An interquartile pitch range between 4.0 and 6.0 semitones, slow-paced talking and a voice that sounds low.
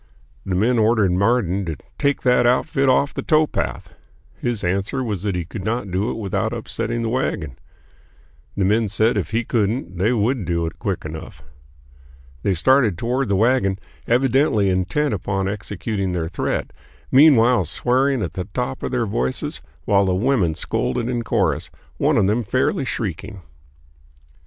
No: average, 4.6 semitones; average, 160 wpm; low, 110 Hz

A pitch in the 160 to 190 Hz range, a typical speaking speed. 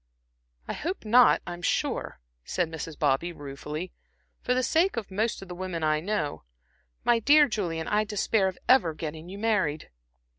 Yes: medium, 185 Hz; average, 170 wpm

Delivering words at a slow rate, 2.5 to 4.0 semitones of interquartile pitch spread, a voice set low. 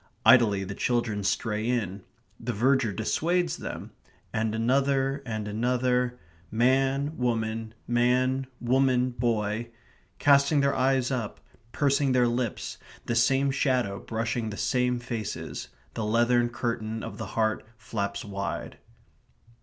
Yes: slow, 120 wpm; average, 2.9 semitones; low, 120 Hz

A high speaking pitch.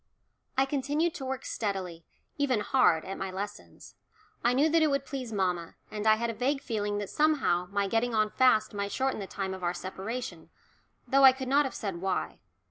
Yes: high, 220 Hz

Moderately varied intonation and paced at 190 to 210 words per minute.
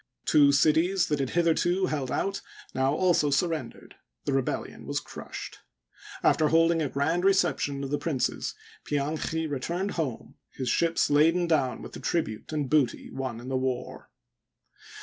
No: average, 3.7 semitones; average, 155 wpm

